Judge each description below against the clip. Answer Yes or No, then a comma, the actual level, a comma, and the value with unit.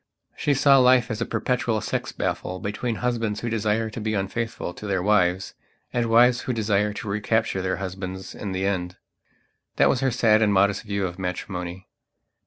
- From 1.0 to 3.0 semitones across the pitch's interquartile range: No, average, 3.4 semitones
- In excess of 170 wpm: Yes, average, 185 wpm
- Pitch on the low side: Yes, low, 105 Hz